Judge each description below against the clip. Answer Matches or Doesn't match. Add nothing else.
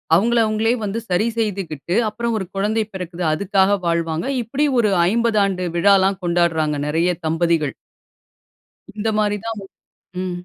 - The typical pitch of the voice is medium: Doesn't match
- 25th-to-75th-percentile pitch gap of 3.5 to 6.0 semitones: Matches